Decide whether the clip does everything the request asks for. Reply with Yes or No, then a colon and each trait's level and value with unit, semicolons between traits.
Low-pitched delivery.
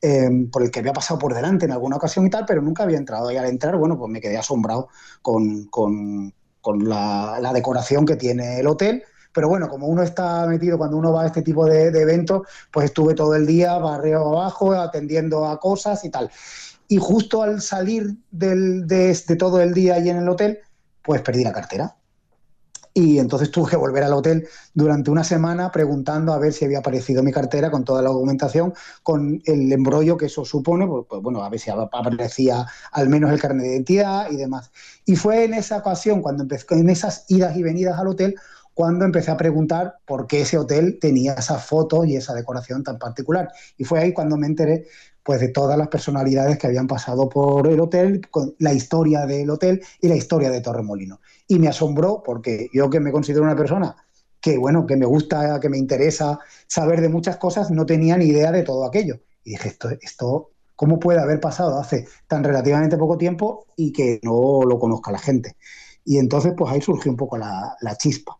No: medium, 155 Hz